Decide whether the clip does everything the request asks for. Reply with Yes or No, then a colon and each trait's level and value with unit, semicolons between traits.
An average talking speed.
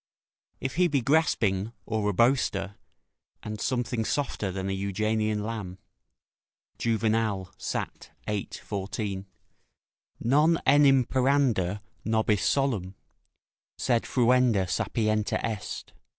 No: slow, 100 wpm